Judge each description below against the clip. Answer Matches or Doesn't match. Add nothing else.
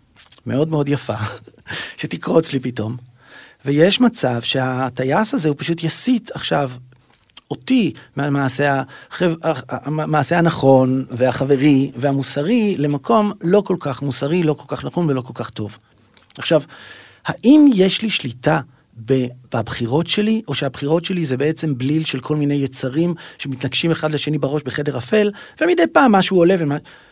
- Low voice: Doesn't match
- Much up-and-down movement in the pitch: Doesn't match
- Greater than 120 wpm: Matches